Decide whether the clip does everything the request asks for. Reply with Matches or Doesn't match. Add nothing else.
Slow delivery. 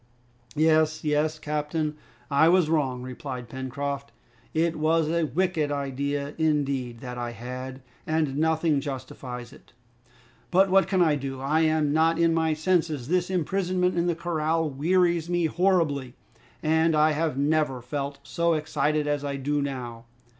Doesn't match